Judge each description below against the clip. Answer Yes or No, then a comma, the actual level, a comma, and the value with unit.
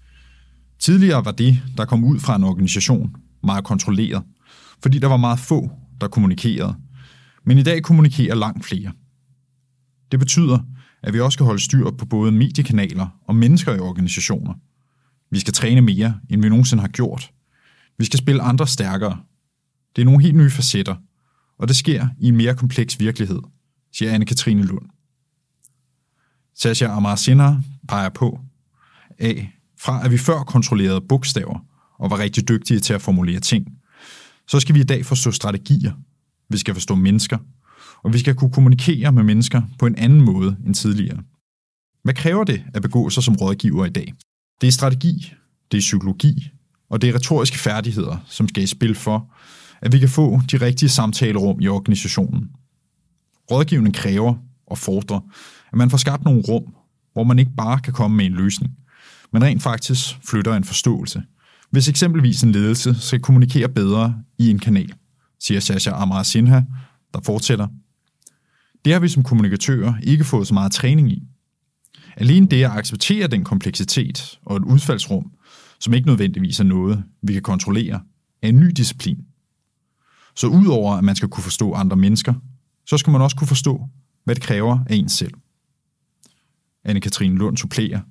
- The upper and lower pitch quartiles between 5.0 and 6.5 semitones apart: No, average, 4.6 semitones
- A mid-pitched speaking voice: No, low, 120 Hz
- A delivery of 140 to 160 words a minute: No, average, 170 wpm